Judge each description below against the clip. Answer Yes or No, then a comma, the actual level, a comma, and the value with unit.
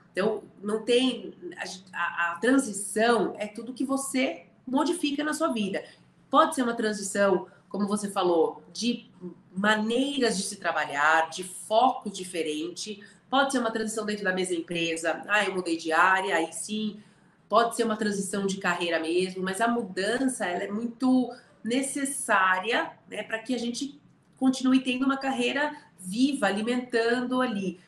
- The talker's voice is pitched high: Yes, high, 210 Hz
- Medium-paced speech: Yes, average, 155 wpm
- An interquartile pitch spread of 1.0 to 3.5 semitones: No, average, 5.1 semitones